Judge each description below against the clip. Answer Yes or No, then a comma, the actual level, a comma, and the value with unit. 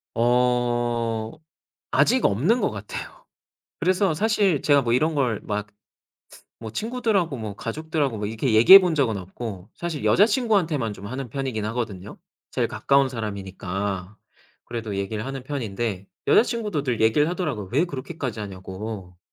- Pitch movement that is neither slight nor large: No, wide, 6.5 semitones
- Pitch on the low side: Yes, low, 120 Hz